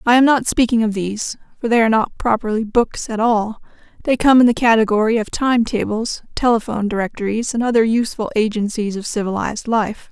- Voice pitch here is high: Yes, high, 225 Hz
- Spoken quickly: No, average, 185 wpm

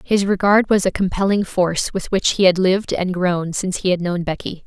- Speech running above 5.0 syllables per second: Yes, 5.5 syllables/s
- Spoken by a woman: Yes, female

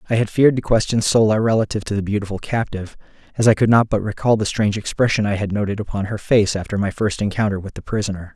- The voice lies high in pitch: No, low, 105 Hz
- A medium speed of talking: No, fast, 235 wpm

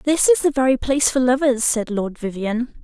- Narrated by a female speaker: Yes, female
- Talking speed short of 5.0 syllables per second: No, 5.6 syllables/s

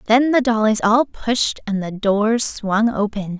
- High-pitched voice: Yes, high, 220 Hz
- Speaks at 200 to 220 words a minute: No, average, 175 wpm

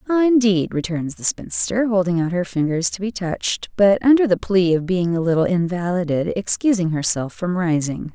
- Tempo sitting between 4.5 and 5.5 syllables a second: Yes, 5.1 syllables/s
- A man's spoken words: No, female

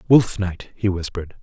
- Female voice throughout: No, male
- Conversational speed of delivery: Yes, average, 170 wpm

